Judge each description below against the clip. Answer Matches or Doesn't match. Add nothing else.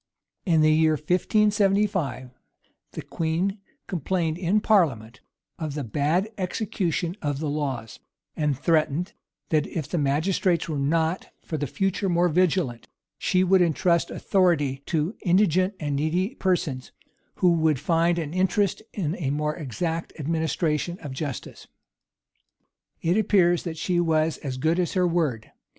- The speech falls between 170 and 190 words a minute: Doesn't match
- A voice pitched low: Doesn't match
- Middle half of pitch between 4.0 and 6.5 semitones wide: Doesn't match